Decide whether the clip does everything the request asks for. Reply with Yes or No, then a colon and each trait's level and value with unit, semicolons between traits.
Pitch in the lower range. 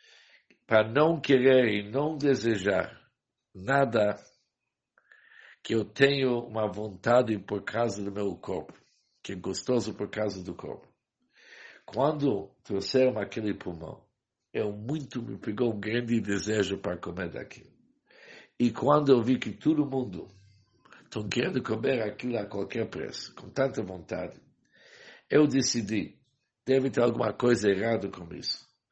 Yes: low, 115 Hz